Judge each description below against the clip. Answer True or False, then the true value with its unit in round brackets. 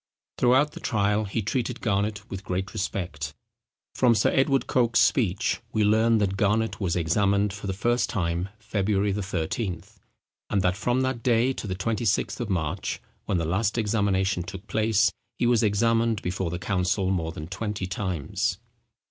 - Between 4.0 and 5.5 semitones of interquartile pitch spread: False (3.3 semitones)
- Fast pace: False (165 wpm)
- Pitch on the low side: True (100 Hz)